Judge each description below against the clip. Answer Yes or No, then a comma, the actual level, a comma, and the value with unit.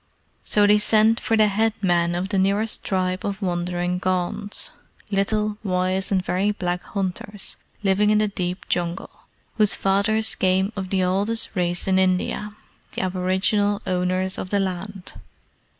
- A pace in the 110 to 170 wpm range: Yes, average, 150 wpm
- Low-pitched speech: No, high, 190 Hz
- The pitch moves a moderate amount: No, narrow, 2.1 semitones